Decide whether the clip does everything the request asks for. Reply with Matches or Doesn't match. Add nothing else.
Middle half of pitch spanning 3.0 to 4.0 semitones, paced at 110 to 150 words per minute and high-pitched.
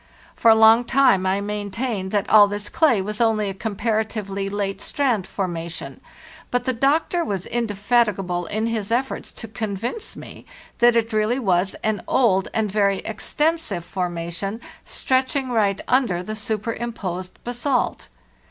Matches